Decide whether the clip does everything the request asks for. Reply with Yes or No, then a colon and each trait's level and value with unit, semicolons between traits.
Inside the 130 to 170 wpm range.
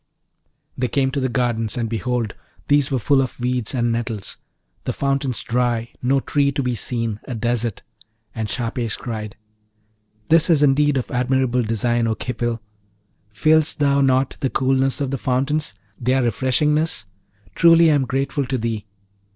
Yes: average, 160 wpm